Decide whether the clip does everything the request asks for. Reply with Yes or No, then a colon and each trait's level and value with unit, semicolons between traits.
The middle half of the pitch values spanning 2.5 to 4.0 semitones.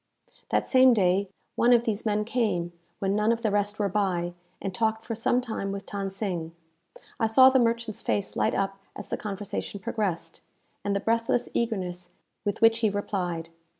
Yes: average, 2.9 semitones